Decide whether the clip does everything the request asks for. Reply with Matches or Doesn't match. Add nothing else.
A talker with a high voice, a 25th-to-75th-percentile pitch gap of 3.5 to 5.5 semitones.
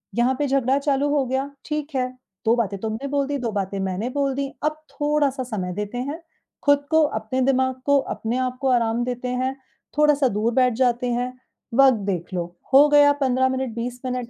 Doesn't match